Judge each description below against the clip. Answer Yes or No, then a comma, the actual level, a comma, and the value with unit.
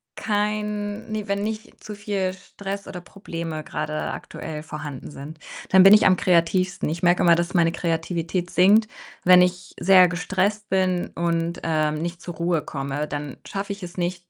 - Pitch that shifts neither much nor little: Yes, average, 3.0 semitones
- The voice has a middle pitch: Yes, medium, 180 Hz